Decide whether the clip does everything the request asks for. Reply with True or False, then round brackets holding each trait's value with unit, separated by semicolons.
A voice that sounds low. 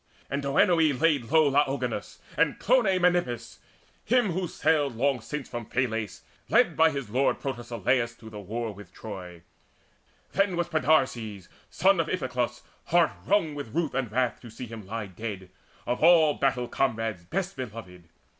True (130 Hz)